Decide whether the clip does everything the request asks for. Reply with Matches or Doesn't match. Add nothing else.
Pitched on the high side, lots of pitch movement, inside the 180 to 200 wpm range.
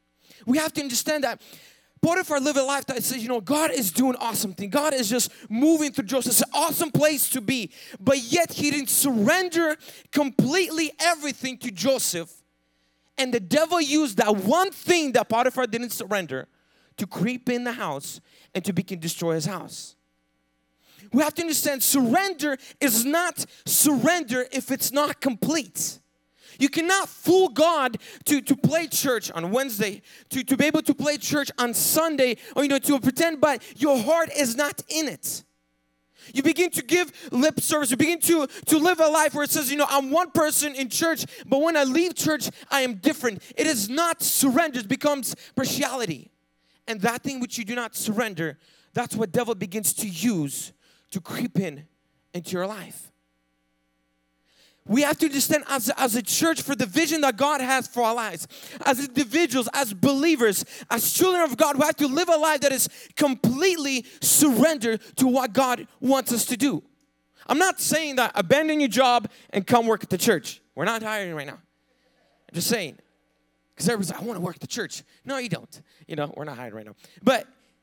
Matches